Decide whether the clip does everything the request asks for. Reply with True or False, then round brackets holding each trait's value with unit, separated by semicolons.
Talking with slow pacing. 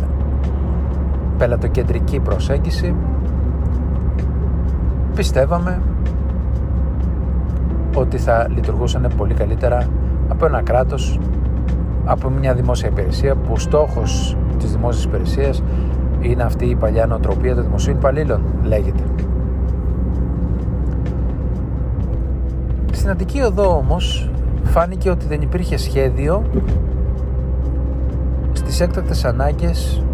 True (85 wpm)